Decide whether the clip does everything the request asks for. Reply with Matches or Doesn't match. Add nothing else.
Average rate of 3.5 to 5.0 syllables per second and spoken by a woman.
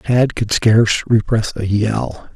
Doesn't match